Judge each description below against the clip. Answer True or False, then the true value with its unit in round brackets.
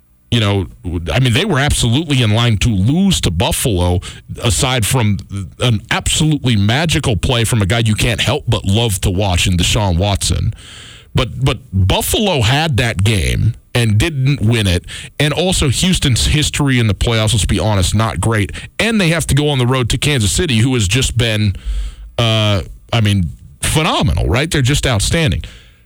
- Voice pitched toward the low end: True (115 Hz)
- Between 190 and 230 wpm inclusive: False (170 wpm)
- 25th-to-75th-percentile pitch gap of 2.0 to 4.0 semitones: False (4.7 semitones)